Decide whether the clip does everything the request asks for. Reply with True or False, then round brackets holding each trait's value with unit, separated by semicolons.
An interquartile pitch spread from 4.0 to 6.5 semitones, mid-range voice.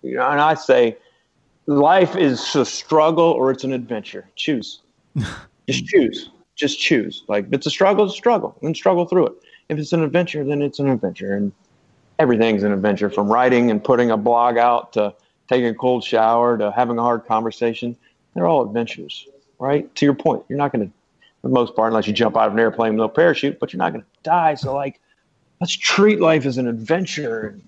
False (5.5 semitones; 130 Hz)